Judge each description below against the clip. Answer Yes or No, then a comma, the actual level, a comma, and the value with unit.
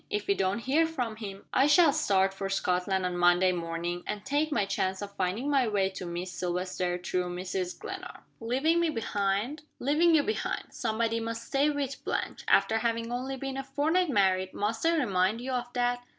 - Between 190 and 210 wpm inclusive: Yes, average, 195 wpm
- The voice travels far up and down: Yes, wide, 6.3 semitones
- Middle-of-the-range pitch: No, high, 220 Hz